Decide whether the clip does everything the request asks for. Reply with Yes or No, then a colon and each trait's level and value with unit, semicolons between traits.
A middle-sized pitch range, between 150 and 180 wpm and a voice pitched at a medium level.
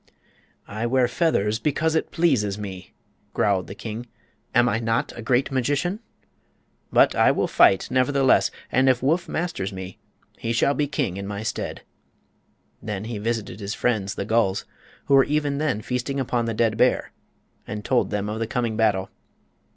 No: average, 4.4 semitones; average, 170 wpm; low, 115 Hz